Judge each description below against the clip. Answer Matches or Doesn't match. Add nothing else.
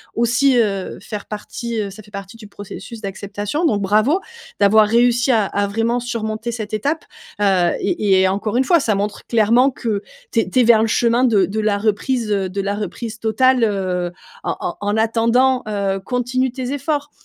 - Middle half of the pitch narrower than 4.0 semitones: Matches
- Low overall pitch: Doesn't match